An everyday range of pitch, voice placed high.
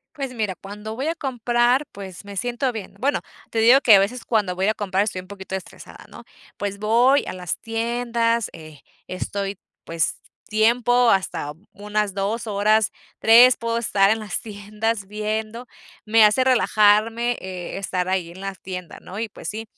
Yes: average, 3.1 semitones; high, 215 Hz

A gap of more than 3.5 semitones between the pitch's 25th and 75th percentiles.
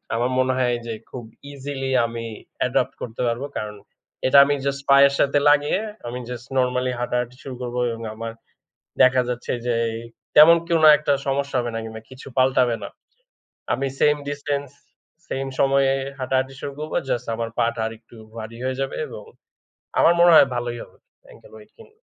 No: average, 2.7 semitones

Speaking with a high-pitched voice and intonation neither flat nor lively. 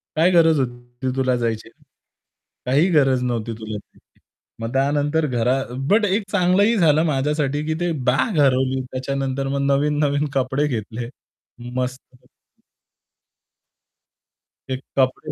No: low, 135 Hz; average, 3.1 semitones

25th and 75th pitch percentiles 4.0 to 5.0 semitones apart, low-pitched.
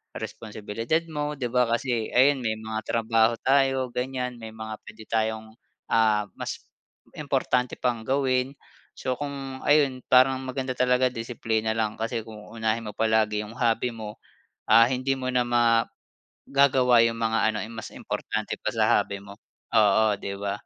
No: average, 2.7 semitones; low, 115 Hz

